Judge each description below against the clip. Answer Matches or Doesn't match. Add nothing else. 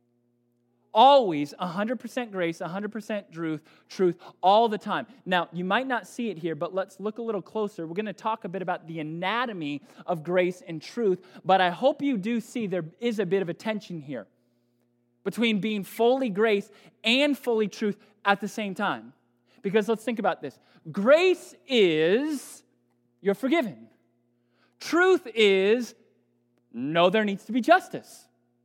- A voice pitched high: Matches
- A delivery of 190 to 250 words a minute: Doesn't match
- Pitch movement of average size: Doesn't match